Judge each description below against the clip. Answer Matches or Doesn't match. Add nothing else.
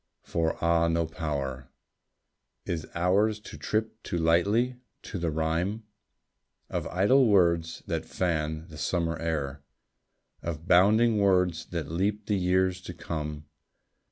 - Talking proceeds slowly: Matches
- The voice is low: Matches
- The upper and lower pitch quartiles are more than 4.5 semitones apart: Doesn't match